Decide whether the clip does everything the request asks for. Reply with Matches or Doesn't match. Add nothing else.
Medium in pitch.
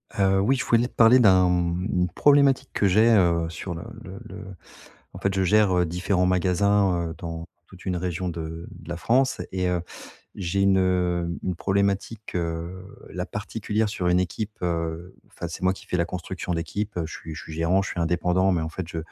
Doesn't match